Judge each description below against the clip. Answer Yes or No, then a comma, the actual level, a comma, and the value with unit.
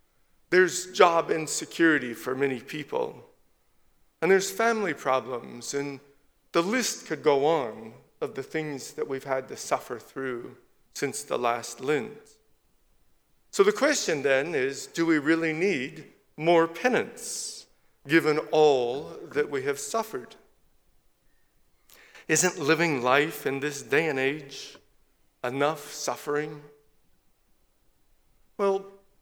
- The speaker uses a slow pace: Yes, slow, 115 wpm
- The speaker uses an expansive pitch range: Yes, wide, 6.3 semitones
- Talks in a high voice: No, medium, 155 Hz